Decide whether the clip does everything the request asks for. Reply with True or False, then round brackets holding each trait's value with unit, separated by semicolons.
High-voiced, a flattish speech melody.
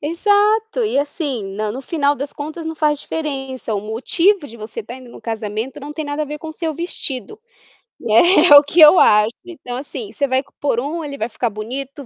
False (280 Hz; 4.9 semitones)